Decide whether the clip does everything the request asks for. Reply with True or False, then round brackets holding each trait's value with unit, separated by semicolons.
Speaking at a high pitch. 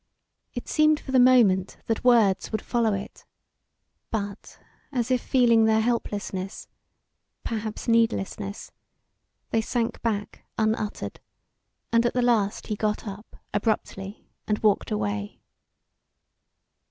True (220 Hz)